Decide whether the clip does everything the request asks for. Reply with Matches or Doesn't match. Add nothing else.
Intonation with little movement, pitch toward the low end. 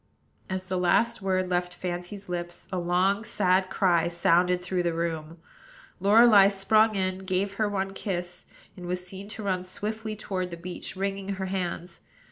Doesn't match